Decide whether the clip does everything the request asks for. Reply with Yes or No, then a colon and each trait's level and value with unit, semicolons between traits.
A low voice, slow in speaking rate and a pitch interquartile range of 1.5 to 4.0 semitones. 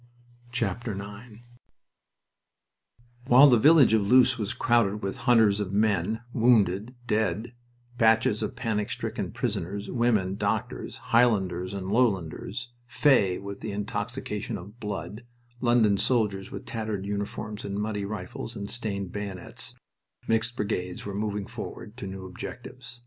Yes: low, 105 Hz; slow, 125 wpm; average, 3.0 semitones